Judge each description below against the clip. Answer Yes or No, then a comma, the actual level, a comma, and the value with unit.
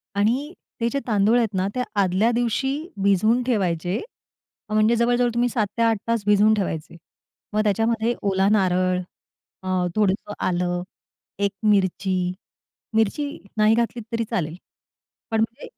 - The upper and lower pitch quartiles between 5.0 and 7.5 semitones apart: No, average, 3.3 semitones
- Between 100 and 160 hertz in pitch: No, high, 215 Hz